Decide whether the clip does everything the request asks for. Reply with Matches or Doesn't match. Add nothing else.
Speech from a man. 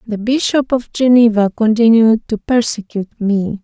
Doesn't match